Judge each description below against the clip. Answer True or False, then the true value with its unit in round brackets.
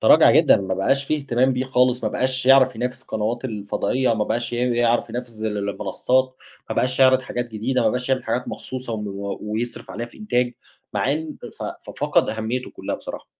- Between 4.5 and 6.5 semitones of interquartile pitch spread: False (2.8 semitones)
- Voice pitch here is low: True (125 Hz)